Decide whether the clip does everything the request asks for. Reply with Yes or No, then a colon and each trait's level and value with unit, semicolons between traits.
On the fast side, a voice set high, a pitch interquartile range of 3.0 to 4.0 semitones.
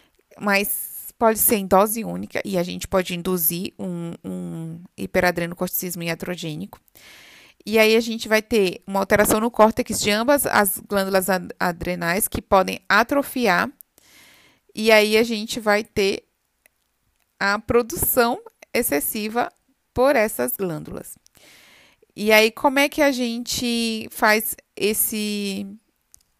No: average, 125 wpm; high, 210 Hz; average, 3.7 semitones